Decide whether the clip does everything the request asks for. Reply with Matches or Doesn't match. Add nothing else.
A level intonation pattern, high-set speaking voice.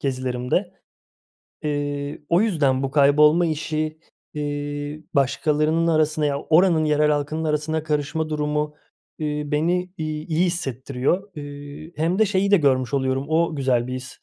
Doesn't match